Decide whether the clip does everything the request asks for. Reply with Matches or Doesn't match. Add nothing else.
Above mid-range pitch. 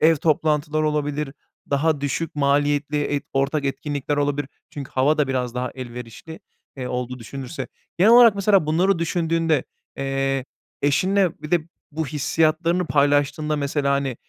Doesn't match